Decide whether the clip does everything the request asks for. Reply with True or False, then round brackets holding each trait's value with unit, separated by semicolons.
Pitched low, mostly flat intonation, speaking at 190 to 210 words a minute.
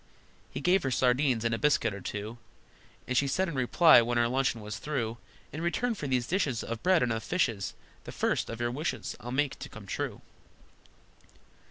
False (125 Hz; 4.4 semitones; 200 wpm)